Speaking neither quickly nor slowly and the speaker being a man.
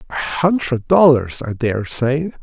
Yes: average, 150 wpm; male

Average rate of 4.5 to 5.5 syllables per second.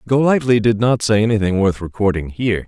No: 6.0 syllables/s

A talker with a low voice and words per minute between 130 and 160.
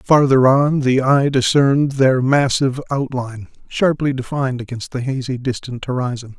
Yes: low, 130 Hz; average, 140 wpm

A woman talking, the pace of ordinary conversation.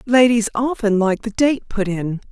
Yes: female; average, 180 wpm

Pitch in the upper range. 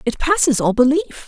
Yes: very high, 270 Hz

